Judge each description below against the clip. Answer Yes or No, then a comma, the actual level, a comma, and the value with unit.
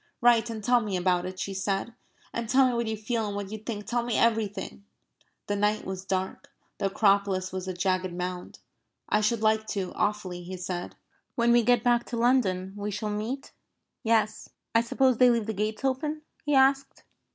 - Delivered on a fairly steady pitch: No, average, 3.7 semitones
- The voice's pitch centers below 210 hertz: No, high, 215 Hz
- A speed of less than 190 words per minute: No, average, 195 wpm